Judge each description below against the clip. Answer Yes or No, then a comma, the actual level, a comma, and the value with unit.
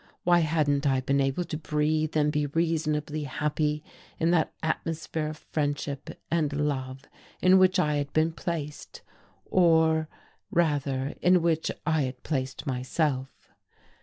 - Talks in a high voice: No, medium, 150 Hz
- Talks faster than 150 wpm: No, slow, 135 wpm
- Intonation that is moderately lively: No, narrow, 2.1 semitones